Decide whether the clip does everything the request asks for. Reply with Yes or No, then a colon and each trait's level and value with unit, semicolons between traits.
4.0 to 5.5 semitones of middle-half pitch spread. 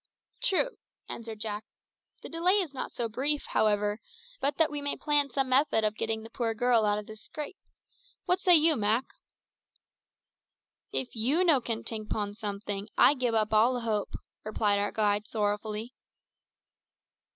Yes: average, 5.1 semitones